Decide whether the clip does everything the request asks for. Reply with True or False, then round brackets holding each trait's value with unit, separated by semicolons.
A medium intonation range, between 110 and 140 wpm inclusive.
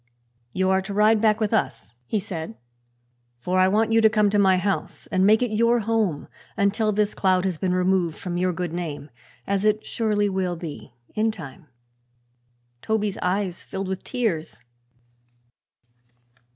False (3.0 semitones; 165 wpm)